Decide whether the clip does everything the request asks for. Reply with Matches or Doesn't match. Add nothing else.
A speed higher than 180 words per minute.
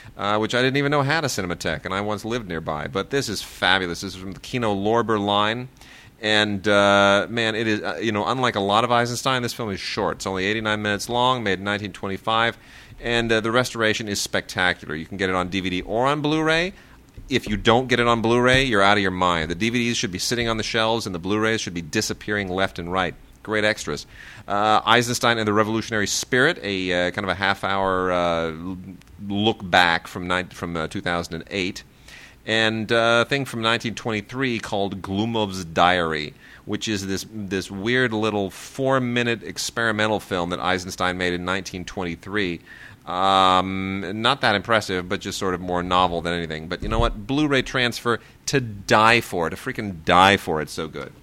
Matches